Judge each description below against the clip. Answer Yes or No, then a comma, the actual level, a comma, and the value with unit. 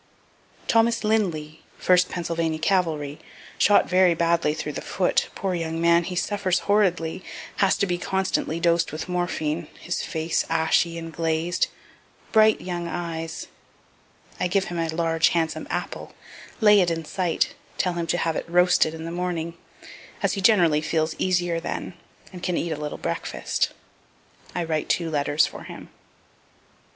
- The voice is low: No, medium, 170 Hz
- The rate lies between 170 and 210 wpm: No, average, 155 wpm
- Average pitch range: No, narrow, 2.0 semitones